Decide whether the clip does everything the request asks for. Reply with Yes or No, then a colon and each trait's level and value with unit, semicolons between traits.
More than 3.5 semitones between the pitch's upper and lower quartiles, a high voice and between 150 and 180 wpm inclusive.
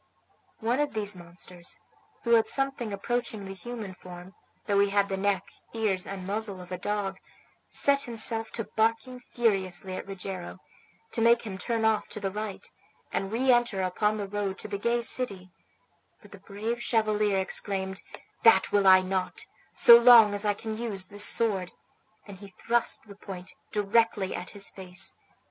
No: average, 2.9 semitones; high, 205 Hz; average, 170 wpm